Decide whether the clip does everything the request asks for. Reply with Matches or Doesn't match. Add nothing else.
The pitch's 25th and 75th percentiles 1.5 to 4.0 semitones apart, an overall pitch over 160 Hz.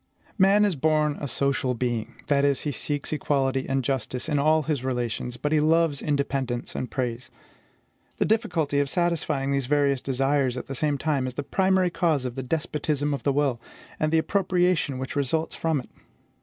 Doesn't match